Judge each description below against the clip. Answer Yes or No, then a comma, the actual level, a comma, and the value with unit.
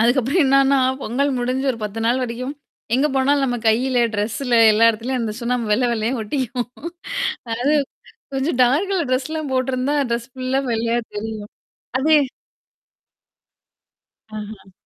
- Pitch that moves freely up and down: No, average, 2.9 semitones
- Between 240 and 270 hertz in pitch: Yes, very high, 250 Hz